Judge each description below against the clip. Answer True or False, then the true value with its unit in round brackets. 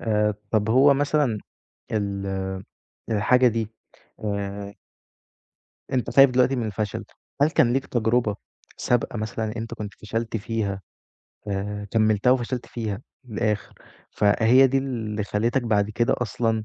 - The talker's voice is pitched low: True (110 Hz)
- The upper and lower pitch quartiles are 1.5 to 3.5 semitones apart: True (2.8 semitones)